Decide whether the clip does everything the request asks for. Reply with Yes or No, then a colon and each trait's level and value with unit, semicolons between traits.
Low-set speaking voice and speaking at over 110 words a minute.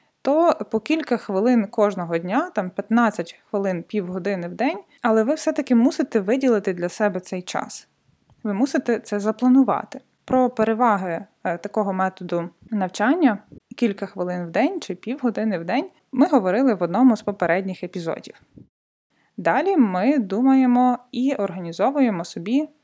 No: high, 220 Hz; average, 135 wpm